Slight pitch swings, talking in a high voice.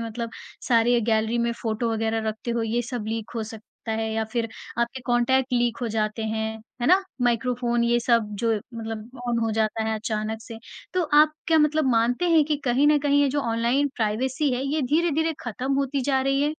No: average, 3.4 semitones; high, 235 Hz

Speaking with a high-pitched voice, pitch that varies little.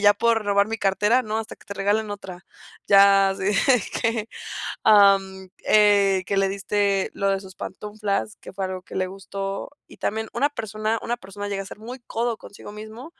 Yes: high, 205 Hz; narrow, 1.9 semitones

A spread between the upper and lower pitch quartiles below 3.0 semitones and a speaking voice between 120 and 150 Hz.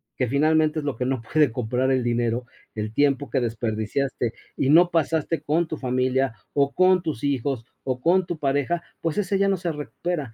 No: average, 4.4 semitones; medium, 140 Hz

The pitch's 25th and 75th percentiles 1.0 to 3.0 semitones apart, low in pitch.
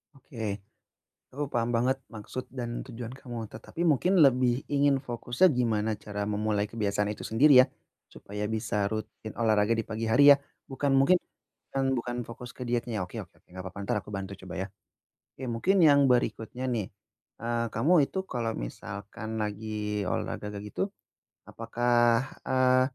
No: average, 3.5 semitones; low, 115 Hz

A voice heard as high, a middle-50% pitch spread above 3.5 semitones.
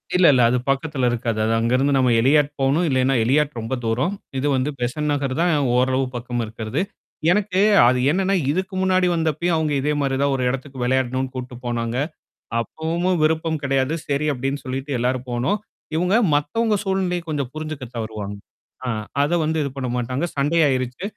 No: medium, 140 Hz; average, 3.9 semitones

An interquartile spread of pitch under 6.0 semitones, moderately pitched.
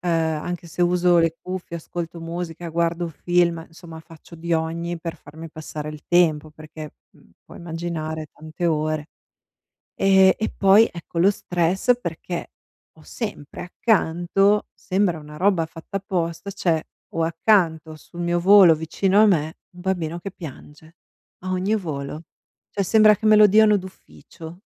Yes: narrow, 2.6 semitones; medium, 170 Hz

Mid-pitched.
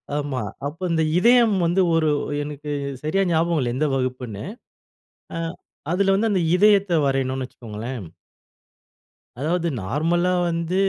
Yes: medium, 160 Hz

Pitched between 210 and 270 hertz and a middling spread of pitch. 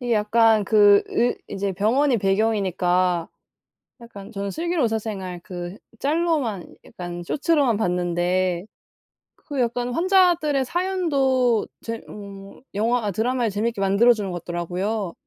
Yes: high, 215 Hz; average, 4.6 semitones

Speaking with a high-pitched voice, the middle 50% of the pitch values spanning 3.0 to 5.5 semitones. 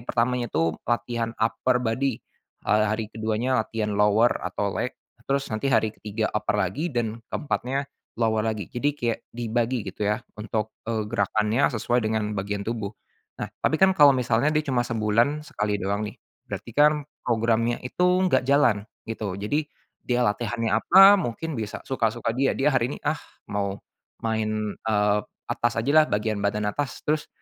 No: low, 115 Hz; average, 3.4 semitones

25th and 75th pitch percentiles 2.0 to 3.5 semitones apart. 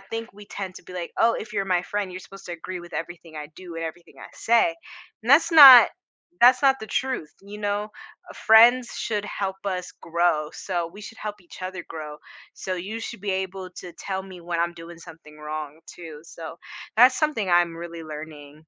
No: average, 4.0 semitones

